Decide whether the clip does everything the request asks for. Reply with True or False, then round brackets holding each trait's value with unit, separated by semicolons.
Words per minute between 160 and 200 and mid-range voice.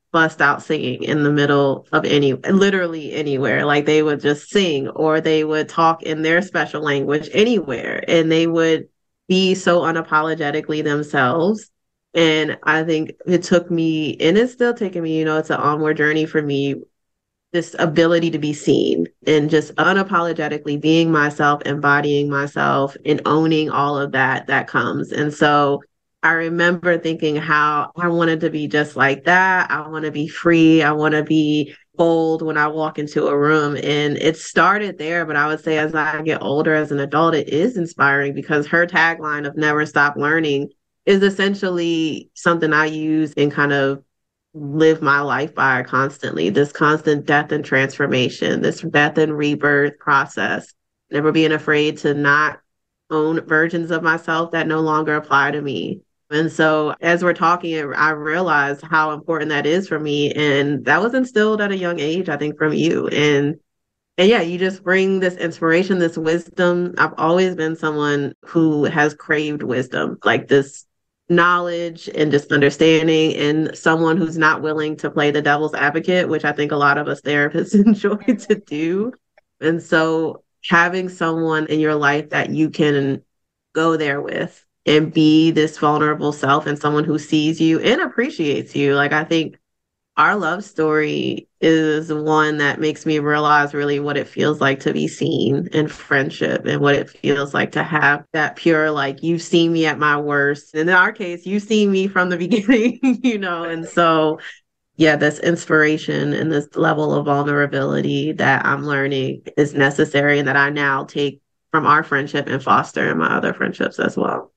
True (175 wpm; 155 Hz)